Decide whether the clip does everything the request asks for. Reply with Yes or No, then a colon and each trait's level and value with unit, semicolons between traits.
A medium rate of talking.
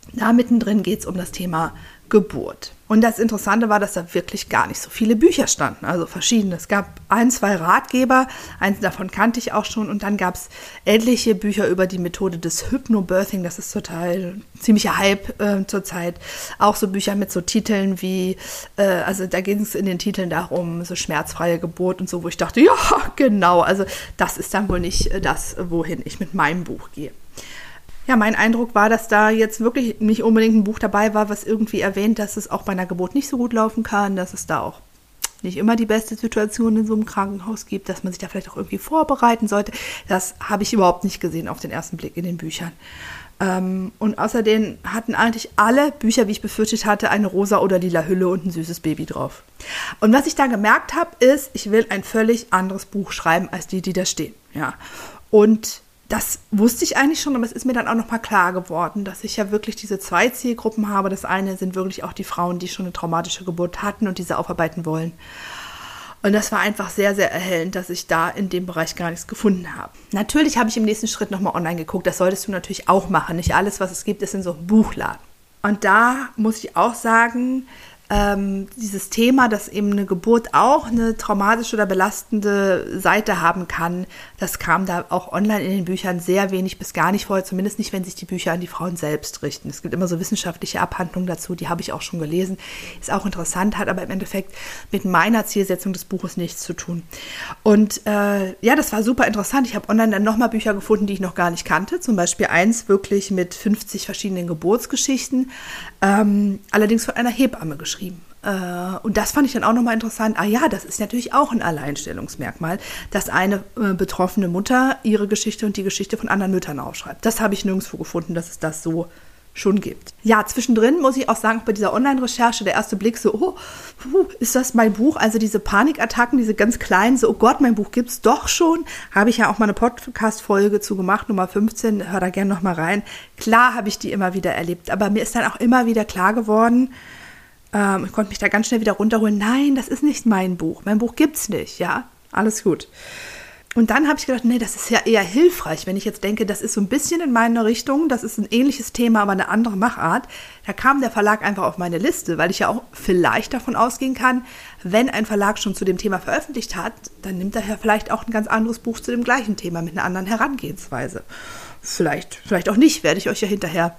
No: fast, 220 wpm